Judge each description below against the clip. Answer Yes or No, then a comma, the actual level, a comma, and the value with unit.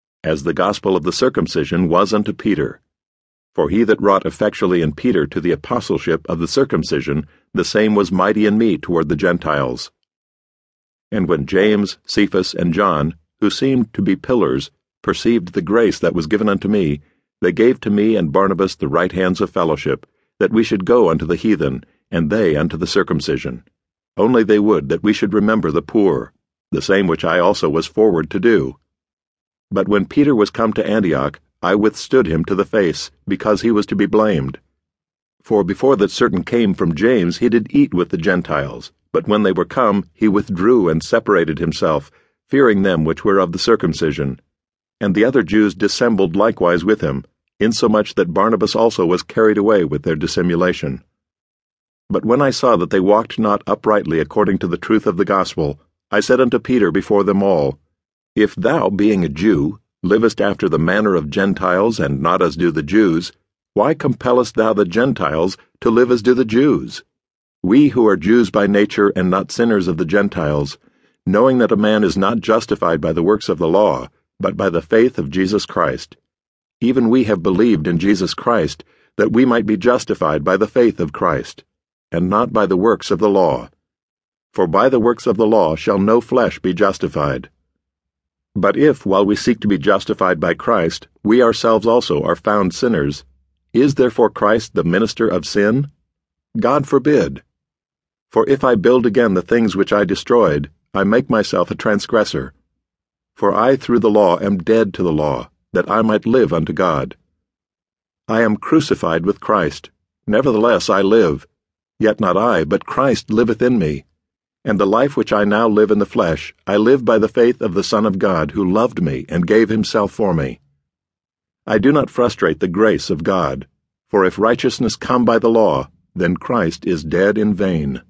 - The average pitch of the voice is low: Yes, low, 100 Hz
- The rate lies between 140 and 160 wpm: No, average, 185 wpm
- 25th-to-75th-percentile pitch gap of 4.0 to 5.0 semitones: Yes, average, 4.6 semitones